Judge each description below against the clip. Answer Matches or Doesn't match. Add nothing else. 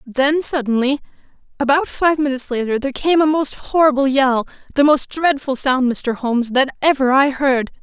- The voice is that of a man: Doesn't match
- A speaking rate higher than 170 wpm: Doesn't match